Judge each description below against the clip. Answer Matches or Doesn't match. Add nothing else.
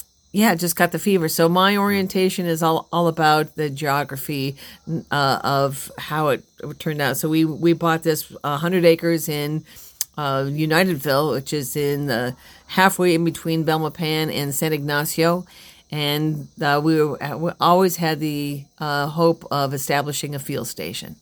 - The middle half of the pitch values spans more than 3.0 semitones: Doesn't match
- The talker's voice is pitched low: Doesn't match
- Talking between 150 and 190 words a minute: Matches